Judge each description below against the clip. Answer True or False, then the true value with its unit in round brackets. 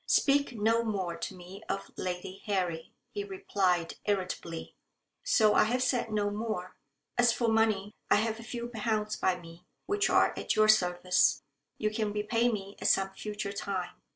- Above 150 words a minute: True (170 wpm)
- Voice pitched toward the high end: True (210 Hz)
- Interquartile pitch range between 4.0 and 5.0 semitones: False (3.5 semitones)